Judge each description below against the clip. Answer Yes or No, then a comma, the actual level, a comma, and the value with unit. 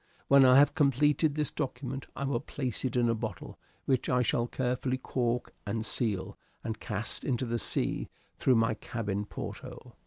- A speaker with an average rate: Yes, average, 175 wpm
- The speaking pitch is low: Yes, low, 125 Hz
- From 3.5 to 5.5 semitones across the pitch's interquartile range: No, average, 2.7 semitones